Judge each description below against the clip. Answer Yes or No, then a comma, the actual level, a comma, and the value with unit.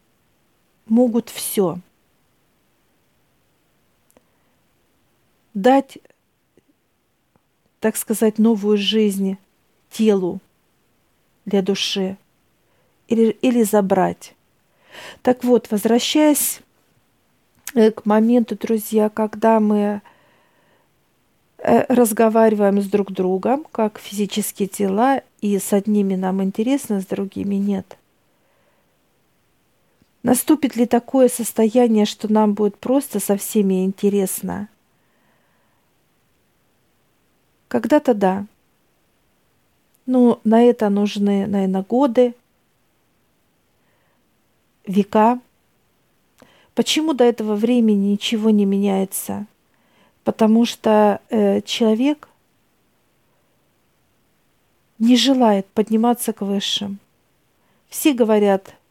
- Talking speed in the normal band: No, slow, 75 wpm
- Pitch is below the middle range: No, high, 215 Hz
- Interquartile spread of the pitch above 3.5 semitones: No, average, 2.9 semitones